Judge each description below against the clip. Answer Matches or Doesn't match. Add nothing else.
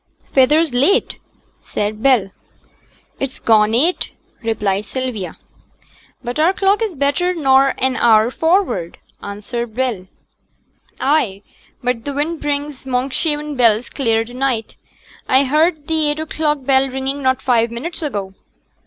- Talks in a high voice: Matches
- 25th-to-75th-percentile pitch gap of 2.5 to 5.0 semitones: Matches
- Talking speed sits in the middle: Doesn't match